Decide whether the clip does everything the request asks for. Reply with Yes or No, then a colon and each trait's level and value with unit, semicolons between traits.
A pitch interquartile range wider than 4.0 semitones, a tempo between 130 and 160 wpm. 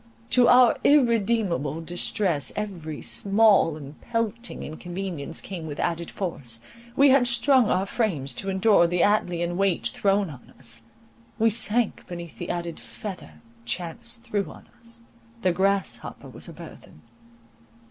Yes: wide, 5.4 semitones; slow, 135 wpm